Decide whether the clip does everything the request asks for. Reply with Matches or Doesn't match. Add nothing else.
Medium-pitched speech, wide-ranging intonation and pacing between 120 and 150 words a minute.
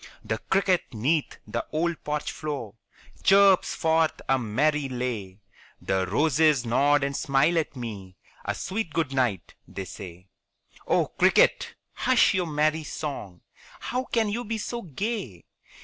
Matches